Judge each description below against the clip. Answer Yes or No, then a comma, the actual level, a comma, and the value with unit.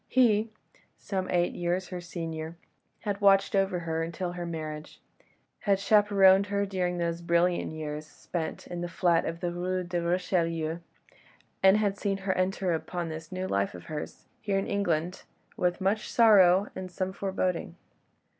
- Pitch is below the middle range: No, medium, 180 Hz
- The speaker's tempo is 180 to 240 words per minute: No, average, 160 wpm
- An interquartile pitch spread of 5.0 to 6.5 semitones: No, narrow, 2.6 semitones